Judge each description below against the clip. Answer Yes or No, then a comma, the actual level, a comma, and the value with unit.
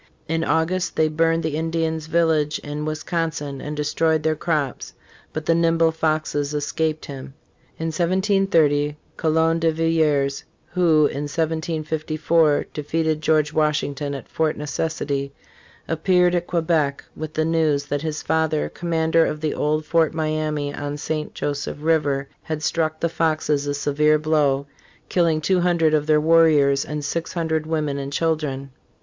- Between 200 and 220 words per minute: No, average, 150 wpm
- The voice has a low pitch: No, medium, 155 Hz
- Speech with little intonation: Yes, narrow, 1.7 semitones